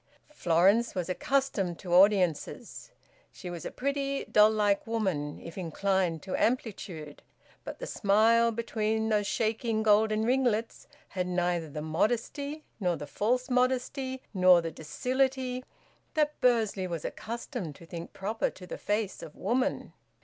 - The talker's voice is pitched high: Yes, high, 215 Hz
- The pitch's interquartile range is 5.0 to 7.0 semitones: Yes, wide, 5.5 semitones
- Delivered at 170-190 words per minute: No, average, 140 wpm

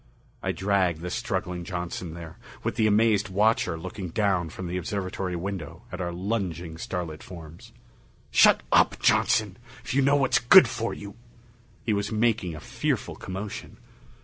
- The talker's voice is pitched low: Yes, very low, 95 Hz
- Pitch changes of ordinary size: Yes, average, 3.7 semitones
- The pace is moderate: Yes, average, 160 wpm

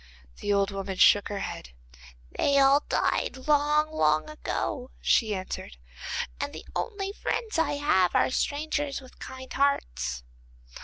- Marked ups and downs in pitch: Yes, wide, 7.2 semitones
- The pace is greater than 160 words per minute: No, average, 140 wpm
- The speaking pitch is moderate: No, very high, 265 Hz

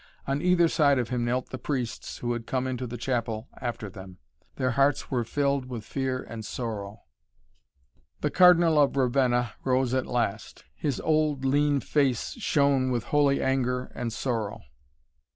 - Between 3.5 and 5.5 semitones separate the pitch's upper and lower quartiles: No, average, 2.8 semitones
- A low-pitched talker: Yes, low, 130 Hz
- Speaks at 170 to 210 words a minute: No, average, 160 wpm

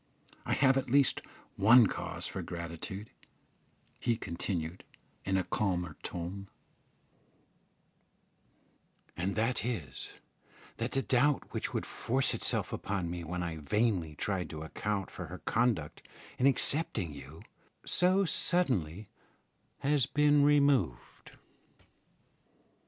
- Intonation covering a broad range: Yes, wide, 7.1 semitones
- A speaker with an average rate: No, slow, 115 wpm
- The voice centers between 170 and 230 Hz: No, low, 100 Hz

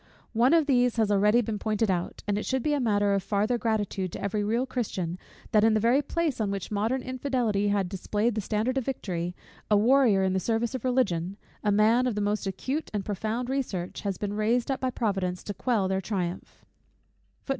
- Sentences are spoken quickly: Yes, fast, 210 wpm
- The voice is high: Yes, high, 215 Hz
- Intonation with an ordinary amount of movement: Yes, average, 3.7 semitones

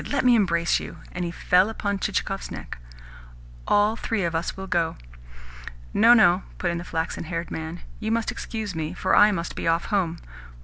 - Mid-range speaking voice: Yes, medium, 180 Hz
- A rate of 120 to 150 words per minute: No, average, 190 wpm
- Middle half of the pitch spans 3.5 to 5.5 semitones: Yes, average, 3.8 semitones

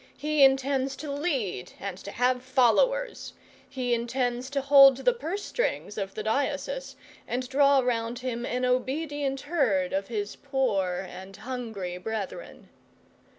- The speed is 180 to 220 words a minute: No, average, 140 wpm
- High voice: Yes, very high, 255 Hz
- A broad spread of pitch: No, average, 4.1 semitones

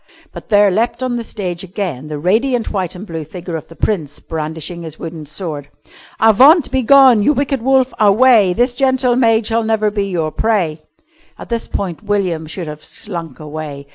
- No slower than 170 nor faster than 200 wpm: Yes, average, 180 wpm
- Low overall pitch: No, high, 200 Hz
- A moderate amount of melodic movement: No, wide, 6.4 semitones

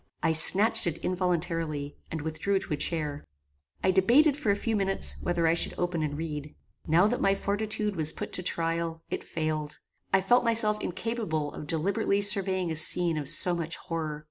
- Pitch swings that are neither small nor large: Yes, average, 4.0 semitones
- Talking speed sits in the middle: Yes, average, 185 wpm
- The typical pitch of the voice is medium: Yes, medium, 175 Hz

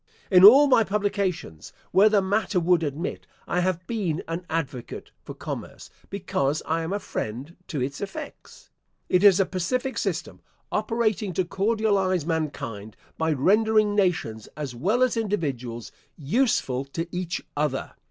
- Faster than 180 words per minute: No, average, 145 wpm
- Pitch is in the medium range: Yes, medium, 180 Hz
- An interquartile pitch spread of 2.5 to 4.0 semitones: No, wide, 5.5 semitones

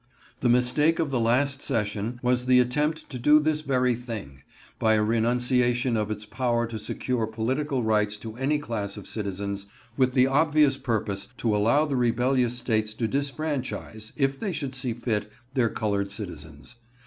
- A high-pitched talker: No, low, 120 Hz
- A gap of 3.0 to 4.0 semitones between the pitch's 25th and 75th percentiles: Yes, average, 3.7 semitones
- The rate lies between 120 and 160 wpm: No, average, 170 wpm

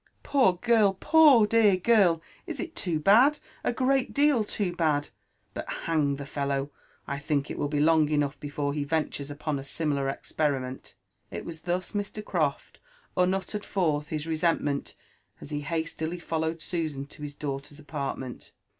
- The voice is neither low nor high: Yes, medium, 160 Hz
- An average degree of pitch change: Yes, average, 4.9 semitones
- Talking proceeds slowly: No, average, 170 wpm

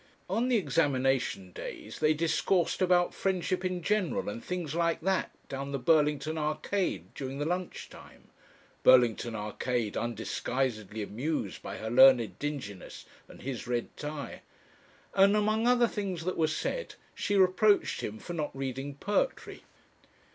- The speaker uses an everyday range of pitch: No, wide, 6.3 semitones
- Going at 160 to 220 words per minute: No, average, 140 wpm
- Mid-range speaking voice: Yes, medium, 155 Hz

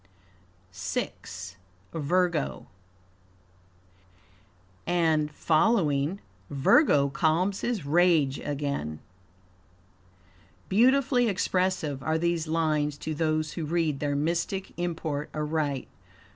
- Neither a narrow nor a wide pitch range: Yes, average, 3.4 semitones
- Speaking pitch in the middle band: Yes, medium, 155 Hz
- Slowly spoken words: Yes, slow, 80 wpm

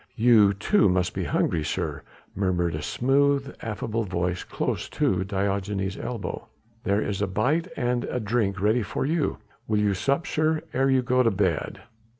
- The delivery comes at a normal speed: Yes, average, 165 wpm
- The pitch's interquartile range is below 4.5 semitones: No, average, 4.8 semitones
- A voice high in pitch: No, low, 105 Hz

